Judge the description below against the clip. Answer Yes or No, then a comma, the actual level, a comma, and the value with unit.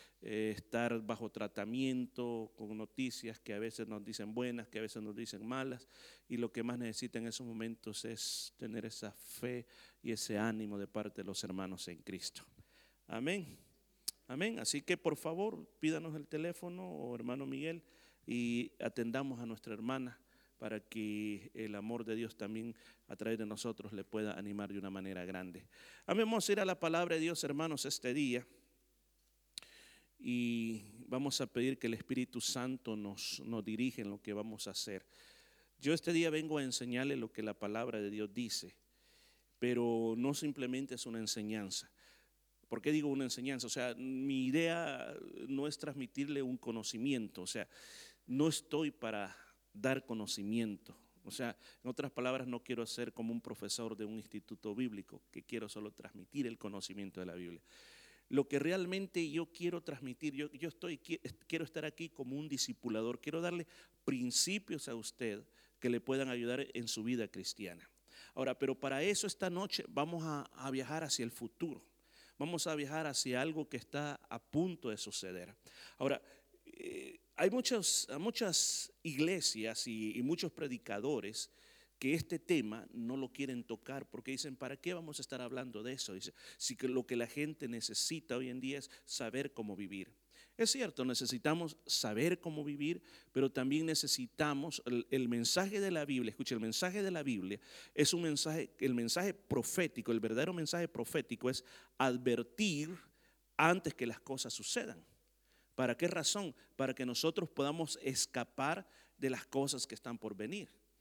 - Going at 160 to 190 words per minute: Yes, average, 170 wpm